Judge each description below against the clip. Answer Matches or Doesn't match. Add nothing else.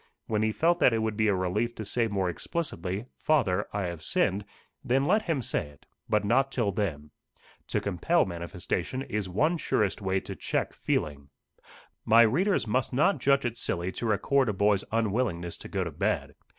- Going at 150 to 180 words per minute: Doesn't match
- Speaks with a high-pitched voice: Doesn't match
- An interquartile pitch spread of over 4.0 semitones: Matches